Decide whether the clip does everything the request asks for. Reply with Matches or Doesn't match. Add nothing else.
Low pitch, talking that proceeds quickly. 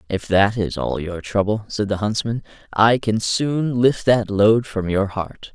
Doesn't match